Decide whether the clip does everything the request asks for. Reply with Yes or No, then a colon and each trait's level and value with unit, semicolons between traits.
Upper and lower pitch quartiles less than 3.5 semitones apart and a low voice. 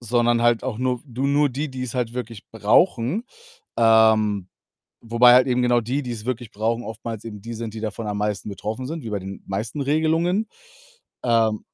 Yes: average, 2.7 semitones; low, 115 Hz